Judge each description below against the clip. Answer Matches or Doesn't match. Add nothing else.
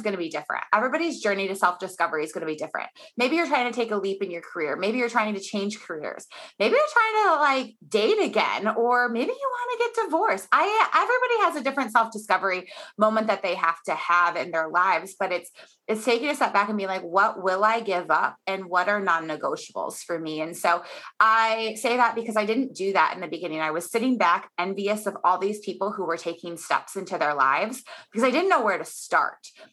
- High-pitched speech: Matches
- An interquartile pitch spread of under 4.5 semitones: Doesn't match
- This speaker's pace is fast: Matches